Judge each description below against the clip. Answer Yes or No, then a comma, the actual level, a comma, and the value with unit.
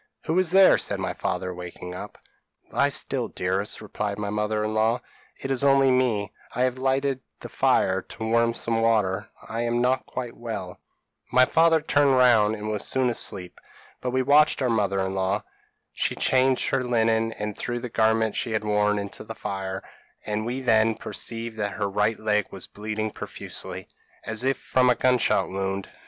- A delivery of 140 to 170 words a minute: No, average, 190 wpm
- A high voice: No, low, 110 Hz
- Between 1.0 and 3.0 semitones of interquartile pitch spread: No, average, 3.4 semitones